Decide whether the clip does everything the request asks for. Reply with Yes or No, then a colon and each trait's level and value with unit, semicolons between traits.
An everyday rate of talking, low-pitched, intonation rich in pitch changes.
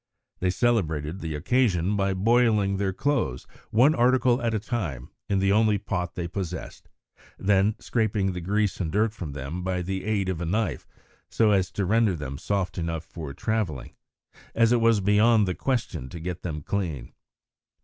No: average, 180 wpm; very low, 95 Hz; average, 4.2 semitones